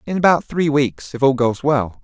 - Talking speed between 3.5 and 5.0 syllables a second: Yes, 4.8 syllables/s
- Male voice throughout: Yes, male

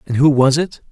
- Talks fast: Yes, fast, 260 wpm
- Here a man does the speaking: Yes, male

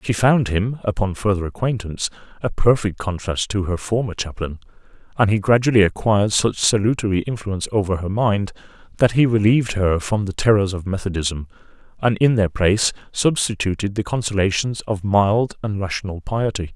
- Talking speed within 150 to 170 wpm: Yes, average, 160 wpm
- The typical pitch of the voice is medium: No, low, 105 Hz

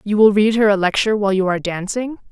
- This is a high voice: Yes, high, 205 Hz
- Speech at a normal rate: No, fast, 260 wpm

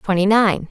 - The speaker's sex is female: Yes, female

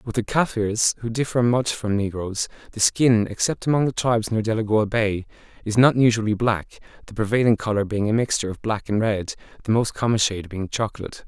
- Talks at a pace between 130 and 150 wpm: No, average, 195 wpm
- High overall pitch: No, low, 110 Hz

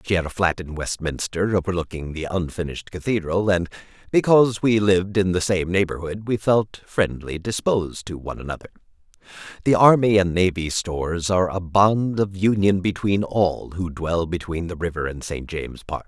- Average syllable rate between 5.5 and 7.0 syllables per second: No, 5.3 syllables/s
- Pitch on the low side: Yes, very low, 90 Hz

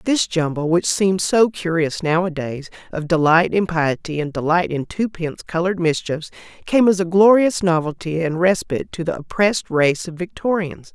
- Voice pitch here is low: No, medium, 170 Hz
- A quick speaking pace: No, average, 155 wpm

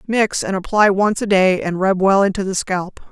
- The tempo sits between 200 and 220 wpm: No, fast, 230 wpm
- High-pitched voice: Yes, high, 195 Hz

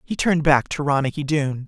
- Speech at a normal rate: No, fast, 215 wpm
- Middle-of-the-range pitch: Yes, medium, 145 Hz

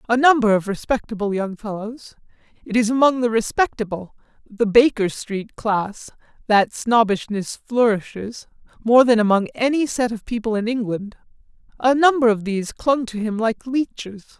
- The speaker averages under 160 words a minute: Yes, average, 145 wpm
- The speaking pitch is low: No, high, 225 Hz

